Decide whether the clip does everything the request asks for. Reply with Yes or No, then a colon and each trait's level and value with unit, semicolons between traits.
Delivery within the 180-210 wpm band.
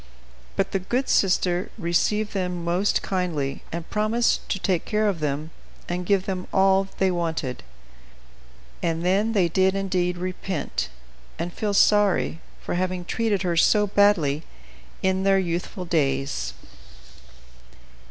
No: slow, 135 wpm